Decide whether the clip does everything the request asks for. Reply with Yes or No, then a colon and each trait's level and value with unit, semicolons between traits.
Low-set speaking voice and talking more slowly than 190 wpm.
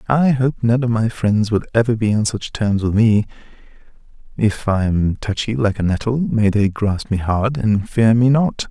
No: low, 110 Hz; fast, 205 wpm